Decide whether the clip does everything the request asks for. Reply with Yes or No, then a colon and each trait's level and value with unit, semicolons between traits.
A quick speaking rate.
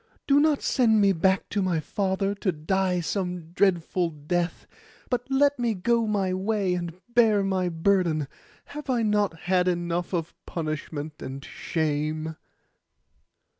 No: average, 140 wpm